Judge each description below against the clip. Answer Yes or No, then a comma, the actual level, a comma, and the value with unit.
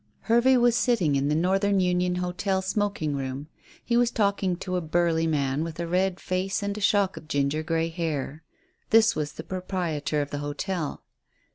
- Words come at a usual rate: Yes, average, 180 wpm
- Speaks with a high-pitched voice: No, medium, 180 Hz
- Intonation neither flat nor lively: Yes, average, 4.3 semitones